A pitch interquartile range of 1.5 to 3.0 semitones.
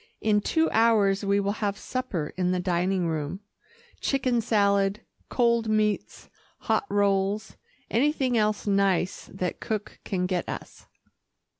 Yes: narrow, 2.6 semitones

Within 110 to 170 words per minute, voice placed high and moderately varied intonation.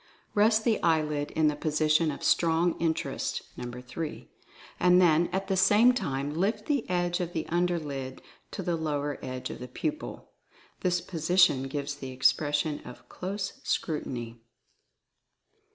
No: average, 150 wpm; medium, 160 Hz; average, 3.8 semitones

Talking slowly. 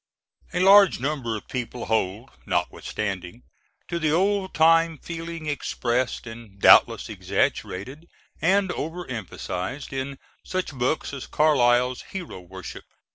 Yes: slow, 120 wpm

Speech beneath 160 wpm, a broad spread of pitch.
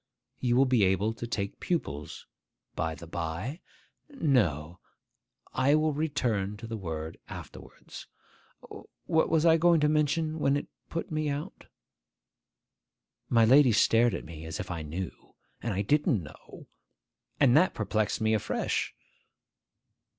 Yes: average, 140 wpm; wide, 8.2 semitones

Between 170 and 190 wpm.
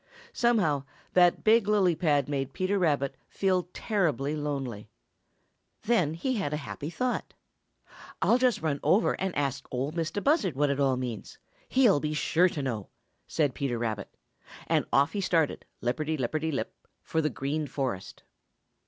No: average, 155 wpm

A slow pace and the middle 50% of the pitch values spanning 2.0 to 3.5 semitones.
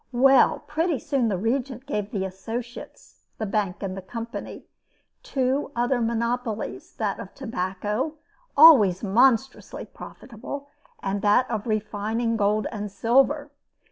No: slow, 125 wpm; average, 4.1 semitones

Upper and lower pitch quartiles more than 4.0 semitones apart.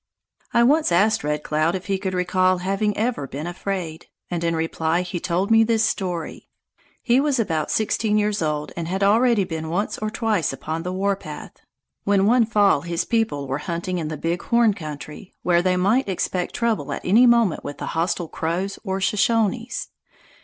Yes: average, 4.4 semitones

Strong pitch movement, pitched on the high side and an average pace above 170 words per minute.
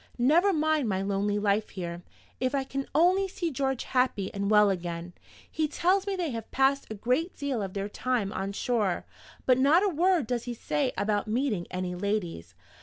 Yes: wide, 6.7 semitones; high, 245 Hz; average, 190 wpm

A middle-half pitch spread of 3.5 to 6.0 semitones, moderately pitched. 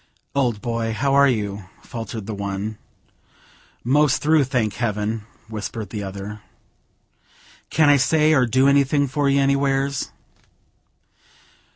No: average, 4.6 semitones; low, 125 Hz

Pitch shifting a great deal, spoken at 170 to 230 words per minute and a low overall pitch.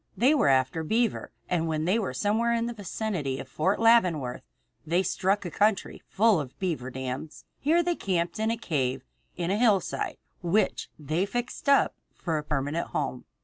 No: wide, 6.5 semitones; average, 180 wpm; medium, 180 Hz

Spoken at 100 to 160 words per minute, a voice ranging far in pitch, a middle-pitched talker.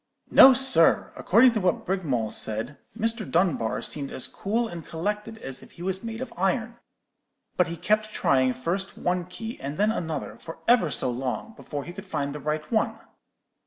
No: average, 185 wpm; wide, 7.0 semitones; medium, 180 Hz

